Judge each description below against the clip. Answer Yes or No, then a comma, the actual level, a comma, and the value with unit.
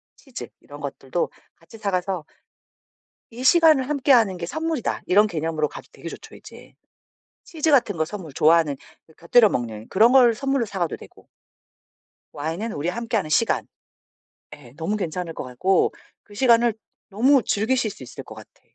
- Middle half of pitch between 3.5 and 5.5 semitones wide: No, wide, 6.9 semitones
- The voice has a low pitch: No, high, 205 Hz